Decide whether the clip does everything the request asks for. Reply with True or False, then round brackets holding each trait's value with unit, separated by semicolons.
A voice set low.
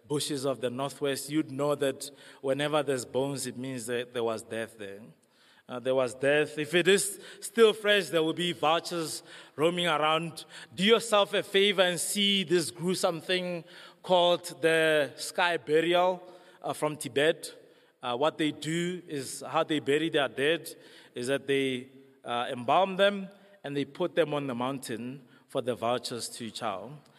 False (150 Hz)